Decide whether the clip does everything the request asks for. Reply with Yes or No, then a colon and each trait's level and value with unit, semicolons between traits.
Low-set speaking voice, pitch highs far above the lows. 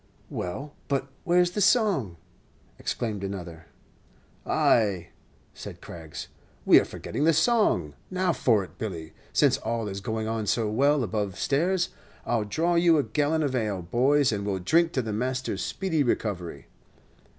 Yes: low, 120 Hz; wide, 7.8 semitones